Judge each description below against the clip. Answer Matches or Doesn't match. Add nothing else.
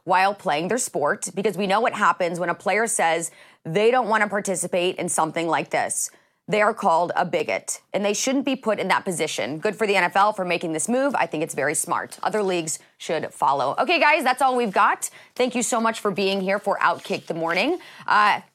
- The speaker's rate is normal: Doesn't match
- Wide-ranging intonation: Doesn't match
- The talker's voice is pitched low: Doesn't match